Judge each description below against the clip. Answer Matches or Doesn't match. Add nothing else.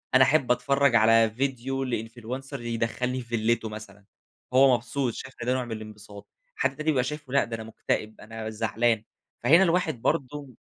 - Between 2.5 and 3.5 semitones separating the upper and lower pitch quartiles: Matches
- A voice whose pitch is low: Matches